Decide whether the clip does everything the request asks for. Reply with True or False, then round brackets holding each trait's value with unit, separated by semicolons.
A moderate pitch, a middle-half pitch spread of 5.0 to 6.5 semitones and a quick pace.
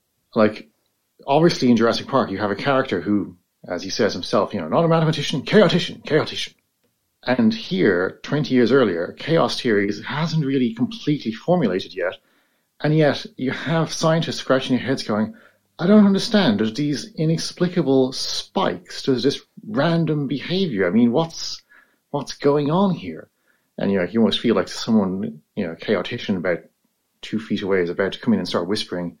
False (145 Hz; 5.5 semitones; 175 wpm)